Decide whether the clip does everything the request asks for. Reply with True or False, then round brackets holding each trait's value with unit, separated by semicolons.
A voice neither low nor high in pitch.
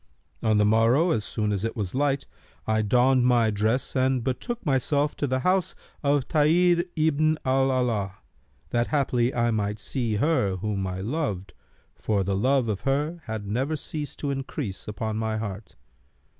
False (125 Hz)